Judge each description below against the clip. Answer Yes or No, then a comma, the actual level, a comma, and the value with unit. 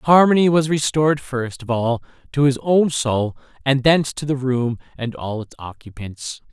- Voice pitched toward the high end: No, low, 130 Hz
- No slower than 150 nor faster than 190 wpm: Yes, average, 175 wpm